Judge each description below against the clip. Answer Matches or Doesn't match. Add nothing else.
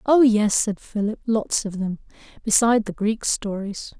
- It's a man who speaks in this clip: Doesn't match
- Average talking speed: Matches